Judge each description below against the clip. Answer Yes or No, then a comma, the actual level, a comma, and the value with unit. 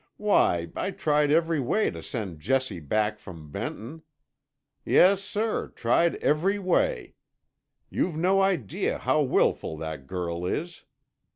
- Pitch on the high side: No, medium, 145 Hz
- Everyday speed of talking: No, slow, 125 wpm